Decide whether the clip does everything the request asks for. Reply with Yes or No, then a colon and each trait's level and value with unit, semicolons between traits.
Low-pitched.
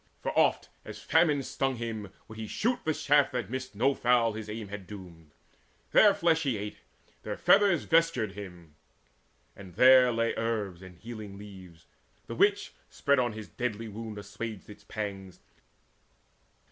Yes: low, 110 Hz